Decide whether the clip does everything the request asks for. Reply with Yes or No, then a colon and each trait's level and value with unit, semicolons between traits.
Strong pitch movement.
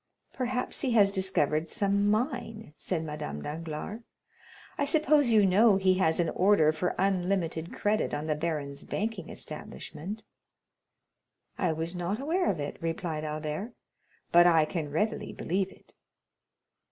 No: average, 5.0 semitones